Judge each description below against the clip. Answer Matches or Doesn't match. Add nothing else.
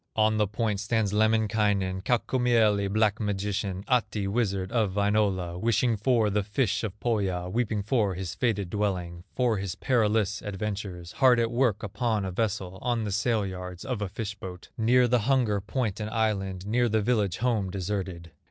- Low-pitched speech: Matches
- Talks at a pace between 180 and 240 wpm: Doesn't match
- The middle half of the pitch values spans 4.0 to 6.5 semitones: Doesn't match